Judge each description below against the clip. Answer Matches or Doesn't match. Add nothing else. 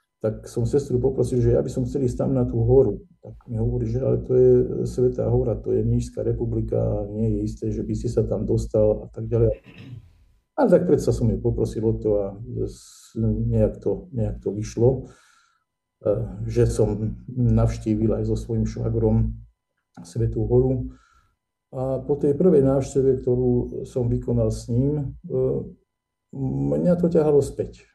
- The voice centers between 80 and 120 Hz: Matches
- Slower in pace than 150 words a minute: Doesn't match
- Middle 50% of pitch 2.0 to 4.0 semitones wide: Matches